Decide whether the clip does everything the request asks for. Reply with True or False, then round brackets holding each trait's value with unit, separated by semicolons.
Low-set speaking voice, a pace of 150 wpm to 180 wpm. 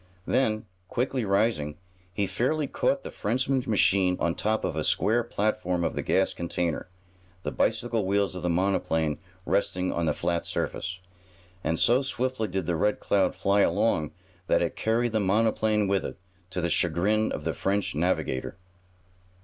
True (100 Hz; 165 wpm)